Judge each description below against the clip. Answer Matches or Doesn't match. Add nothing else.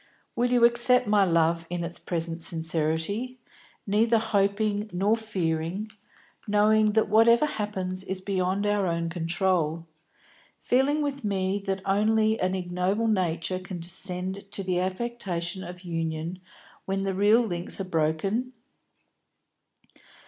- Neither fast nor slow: Doesn't match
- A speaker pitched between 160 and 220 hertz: Matches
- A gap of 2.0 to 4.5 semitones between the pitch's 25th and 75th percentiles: Matches